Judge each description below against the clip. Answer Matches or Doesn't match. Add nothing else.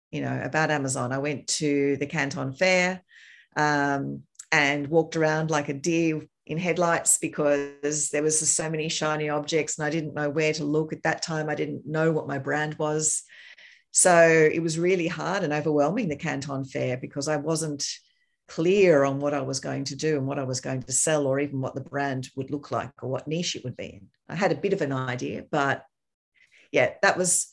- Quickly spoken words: Matches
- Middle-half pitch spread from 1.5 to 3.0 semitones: Matches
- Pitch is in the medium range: Matches